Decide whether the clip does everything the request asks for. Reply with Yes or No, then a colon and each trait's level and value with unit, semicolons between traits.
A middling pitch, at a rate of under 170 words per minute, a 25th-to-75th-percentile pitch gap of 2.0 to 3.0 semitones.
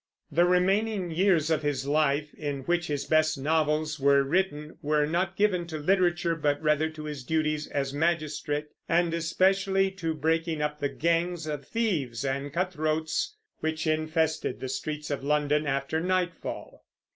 Yes: medium, 155 Hz; average, 155 wpm; average, 2.7 semitones